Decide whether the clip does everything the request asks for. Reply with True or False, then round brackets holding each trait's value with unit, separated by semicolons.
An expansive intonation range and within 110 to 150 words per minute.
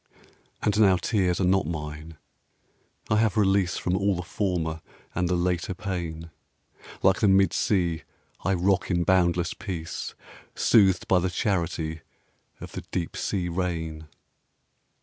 False (2.4 semitones; 140 wpm)